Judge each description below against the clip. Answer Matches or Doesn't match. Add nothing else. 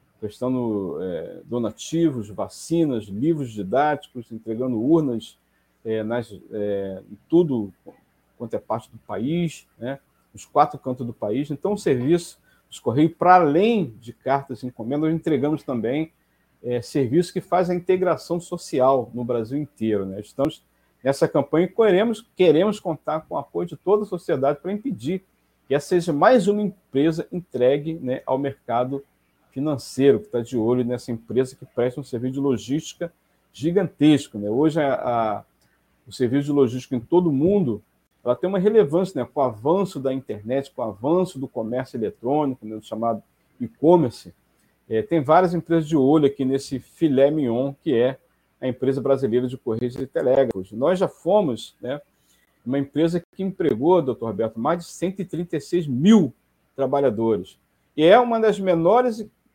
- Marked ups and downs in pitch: Matches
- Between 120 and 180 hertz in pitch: Matches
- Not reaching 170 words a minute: Matches